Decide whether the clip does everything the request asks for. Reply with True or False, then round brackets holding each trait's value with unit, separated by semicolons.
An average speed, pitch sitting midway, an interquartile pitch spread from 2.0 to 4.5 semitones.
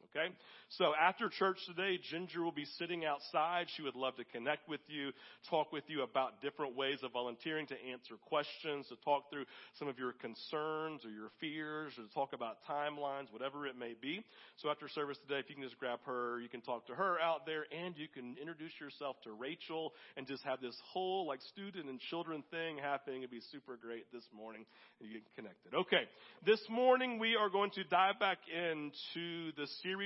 False (210 wpm; 145 Hz; 4.2 semitones)